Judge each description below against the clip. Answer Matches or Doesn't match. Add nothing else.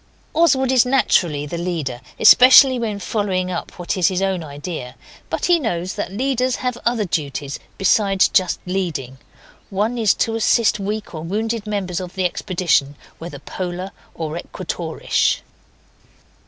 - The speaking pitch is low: Doesn't match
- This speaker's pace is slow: Doesn't match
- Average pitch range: Matches